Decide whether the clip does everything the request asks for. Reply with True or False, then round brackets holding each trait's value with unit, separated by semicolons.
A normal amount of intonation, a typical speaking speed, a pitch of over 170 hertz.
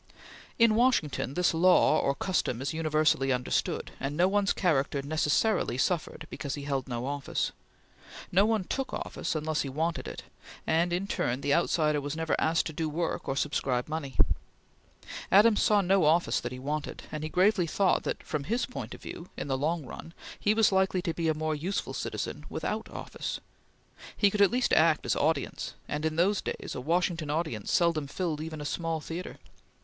False (3.9 semitones; 190 wpm; 160 Hz)